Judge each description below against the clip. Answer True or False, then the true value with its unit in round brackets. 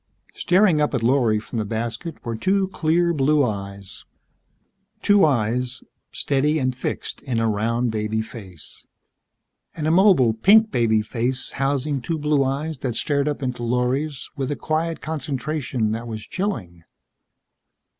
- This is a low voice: True (130 Hz)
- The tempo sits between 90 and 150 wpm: True (145 wpm)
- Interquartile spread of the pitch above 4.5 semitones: True (5.2 semitones)